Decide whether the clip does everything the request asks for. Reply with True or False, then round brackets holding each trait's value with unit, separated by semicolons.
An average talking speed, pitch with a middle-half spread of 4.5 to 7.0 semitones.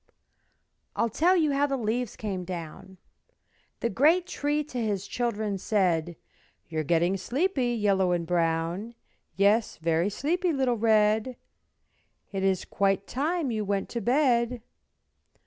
False (130 wpm; 5.3 semitones)